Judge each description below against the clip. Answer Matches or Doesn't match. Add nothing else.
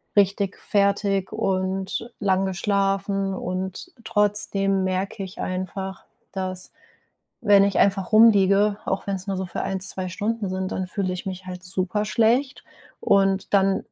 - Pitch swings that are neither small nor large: Doesn't match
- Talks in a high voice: Matches